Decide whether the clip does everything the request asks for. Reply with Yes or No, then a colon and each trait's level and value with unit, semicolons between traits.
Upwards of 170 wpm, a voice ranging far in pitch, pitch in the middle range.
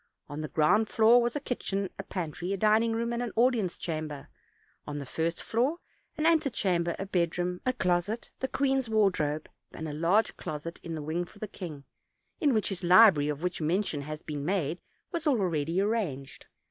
Yes: average, 195 wpm; wide, 6.1 semitones; medium, 180 Hz